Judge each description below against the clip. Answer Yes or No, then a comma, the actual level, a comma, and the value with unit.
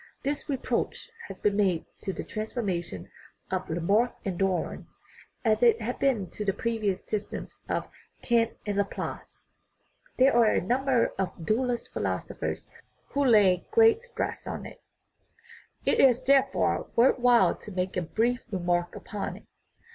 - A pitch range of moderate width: Yes, average, 4.5 semitones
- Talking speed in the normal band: Yes, average, 150 wpm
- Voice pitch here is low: No, high, 220 Hz